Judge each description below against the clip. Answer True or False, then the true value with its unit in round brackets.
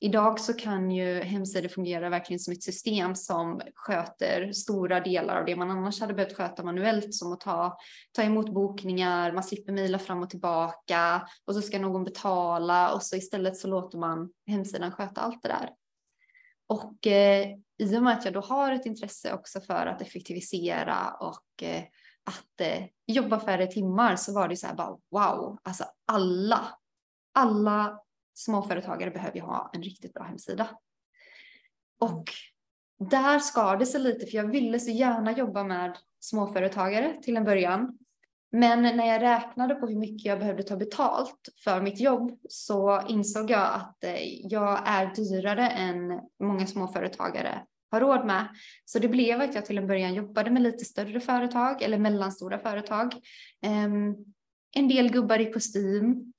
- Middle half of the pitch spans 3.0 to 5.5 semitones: True (3.6 semitones)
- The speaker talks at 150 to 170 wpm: True (165 wpm)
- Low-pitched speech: False (205 Hz)